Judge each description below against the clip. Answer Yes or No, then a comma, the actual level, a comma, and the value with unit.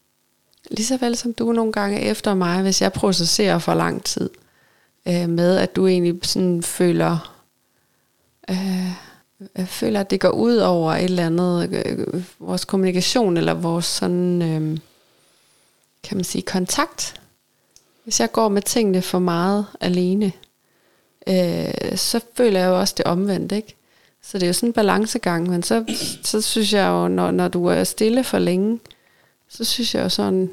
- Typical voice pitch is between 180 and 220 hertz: Yes, medium, 185 Hz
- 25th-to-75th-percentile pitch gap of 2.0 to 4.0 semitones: Yes, average, 3.7 semitones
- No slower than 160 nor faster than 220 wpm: Yes, average, 165 wpm